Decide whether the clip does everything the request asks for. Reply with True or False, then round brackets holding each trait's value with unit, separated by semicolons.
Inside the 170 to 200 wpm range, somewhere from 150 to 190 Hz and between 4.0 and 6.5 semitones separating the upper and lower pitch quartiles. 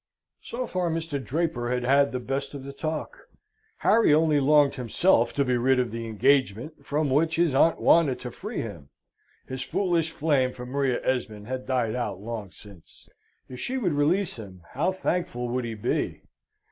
False (180 wpm; 135 Hz; 4.8 semitones)